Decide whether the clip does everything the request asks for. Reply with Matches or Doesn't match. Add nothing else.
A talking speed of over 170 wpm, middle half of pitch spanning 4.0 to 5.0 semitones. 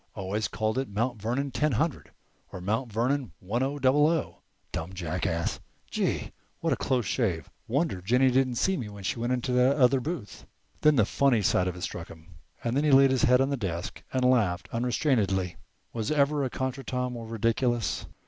Matches